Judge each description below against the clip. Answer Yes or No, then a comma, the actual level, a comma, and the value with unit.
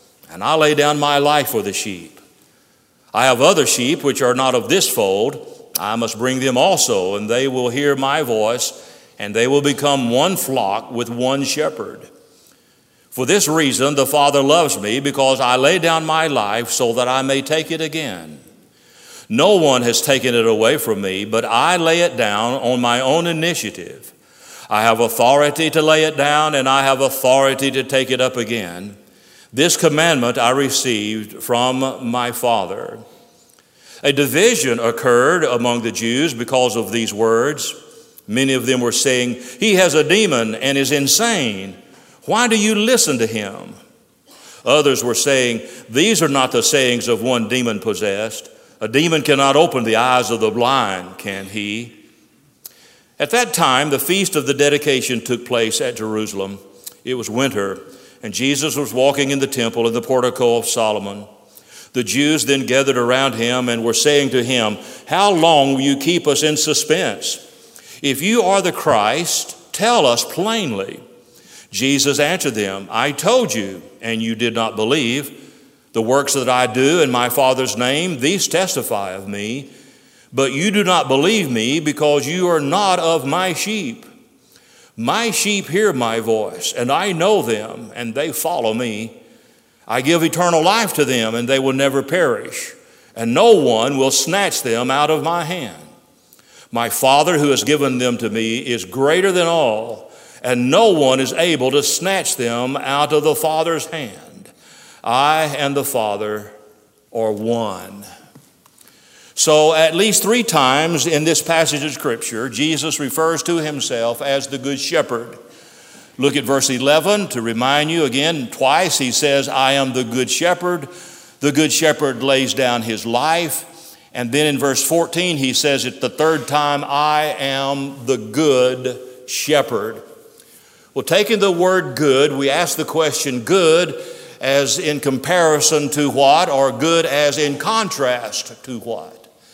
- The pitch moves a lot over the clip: No, average, 4.3 semitones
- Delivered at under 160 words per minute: No, average, 165 wpm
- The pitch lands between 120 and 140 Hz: Yes, low, 135 Hz